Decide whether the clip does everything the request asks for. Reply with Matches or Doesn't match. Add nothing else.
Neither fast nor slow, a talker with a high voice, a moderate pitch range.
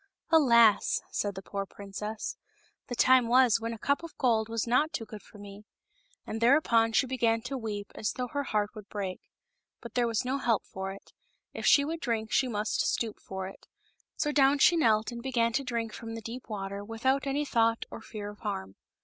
Doesn't match